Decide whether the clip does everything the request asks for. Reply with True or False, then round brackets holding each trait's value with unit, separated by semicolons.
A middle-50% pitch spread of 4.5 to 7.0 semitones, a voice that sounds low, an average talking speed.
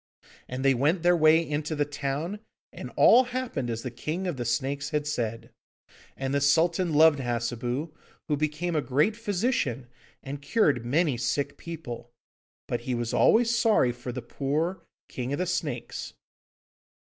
False (4.9 semitones; 145 Hz; 160 wpm)